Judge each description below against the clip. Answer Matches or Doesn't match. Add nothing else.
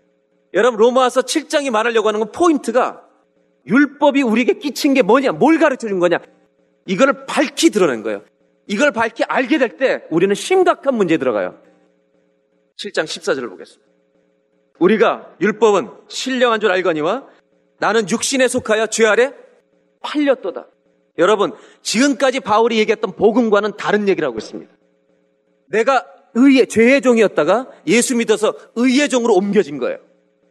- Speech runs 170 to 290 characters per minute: Doesn't match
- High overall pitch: Matches